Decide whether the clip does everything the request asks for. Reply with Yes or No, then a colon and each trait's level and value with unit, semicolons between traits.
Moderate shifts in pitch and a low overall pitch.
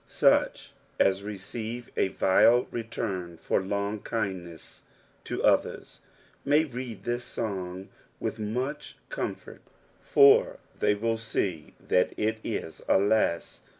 Yes: average, 4.0 semitones; low, 110 Hz